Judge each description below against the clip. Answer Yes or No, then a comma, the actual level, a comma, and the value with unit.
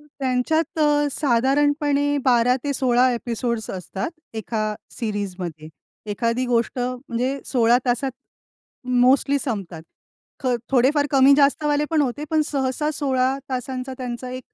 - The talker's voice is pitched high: Yes, very high, 255 Hz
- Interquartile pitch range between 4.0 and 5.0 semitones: No, average, 3.2 semitones